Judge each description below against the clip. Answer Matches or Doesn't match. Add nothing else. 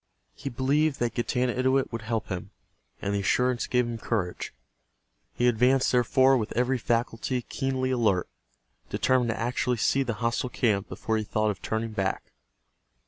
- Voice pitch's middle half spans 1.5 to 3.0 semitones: Matches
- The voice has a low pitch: Matches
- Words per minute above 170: Doesn't match